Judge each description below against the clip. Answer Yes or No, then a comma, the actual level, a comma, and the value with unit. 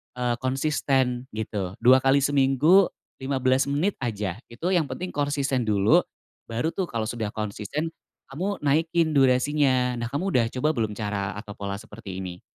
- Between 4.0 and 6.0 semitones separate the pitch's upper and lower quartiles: Yes, average, 4.6 semitones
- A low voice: Yes, low, 130 Hz